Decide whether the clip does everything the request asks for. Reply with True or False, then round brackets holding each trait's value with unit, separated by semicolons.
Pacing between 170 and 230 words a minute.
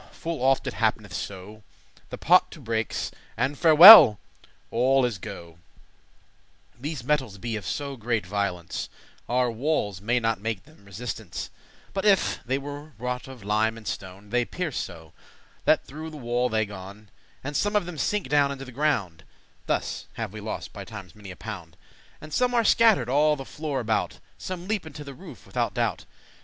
True (185 wpm)